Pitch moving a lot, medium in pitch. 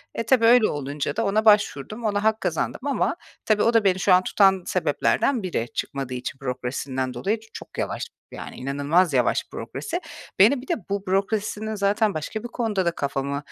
No: wide, 7.4 semitones; high, 195 Hz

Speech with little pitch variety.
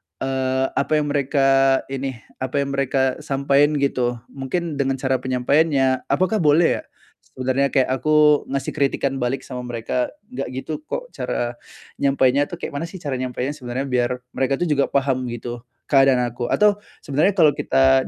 Yes: narrow, 1.9 semitones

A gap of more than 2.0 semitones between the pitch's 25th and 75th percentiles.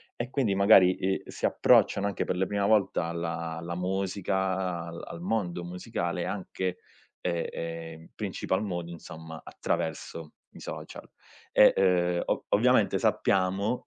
Yes: narrow, 2.5 semitones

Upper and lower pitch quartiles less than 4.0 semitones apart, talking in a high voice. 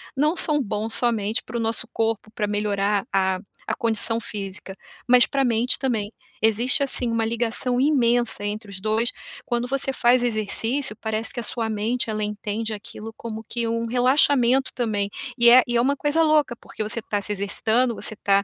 Yes: narrow, 2.6 semitones; high, 230 Hz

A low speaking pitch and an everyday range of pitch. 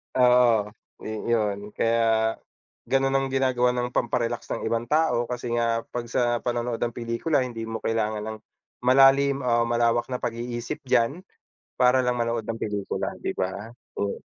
No: low, 120 Hz; narrow, 1.6 semitones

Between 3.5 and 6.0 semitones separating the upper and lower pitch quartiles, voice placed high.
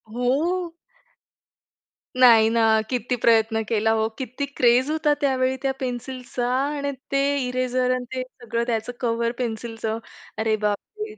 No: average, 2.9 semitones; high, 245 Hz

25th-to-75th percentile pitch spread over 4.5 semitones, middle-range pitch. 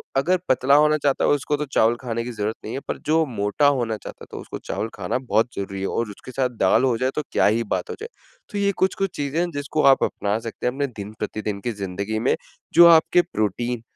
No: average, 5.2 semitones; low, 120 Hz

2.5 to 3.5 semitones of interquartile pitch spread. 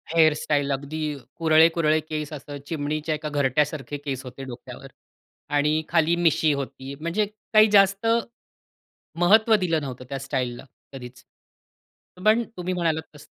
Yes: average, 3.1 semitones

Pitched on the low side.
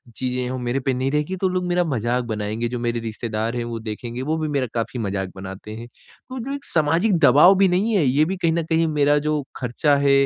Yes: low, 130 Hz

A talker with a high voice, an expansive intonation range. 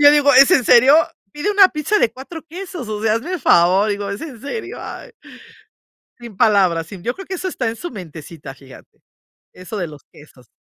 Yes: high, 230 Hz; wide, 8.6 semitones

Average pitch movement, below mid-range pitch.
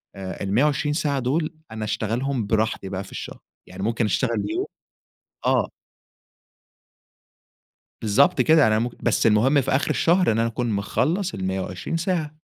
No: wide, 5.9 semitones; low, 120 Hz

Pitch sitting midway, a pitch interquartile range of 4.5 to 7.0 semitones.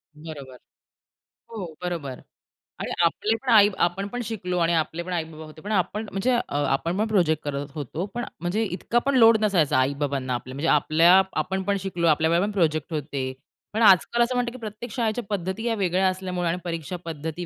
Yes: medium, 180 Hz; average, 5.0 semitones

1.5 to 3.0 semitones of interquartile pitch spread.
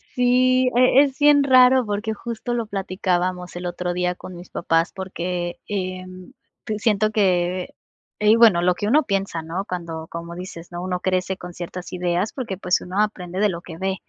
No: average, 3.4 semitones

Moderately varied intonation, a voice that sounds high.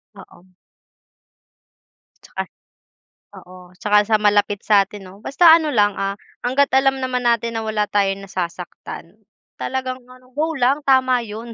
Yes: average, 4.3 semitones; high, 225 Hz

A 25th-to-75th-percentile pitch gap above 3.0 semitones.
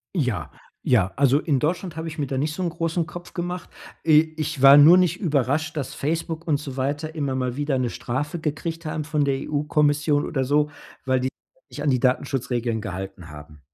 Yes: average, 3.5 semitones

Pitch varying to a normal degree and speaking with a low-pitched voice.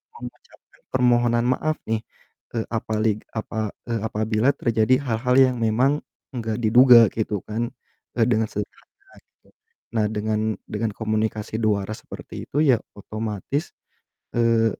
No: narrow, 1.8 semitones; low, 110 Hz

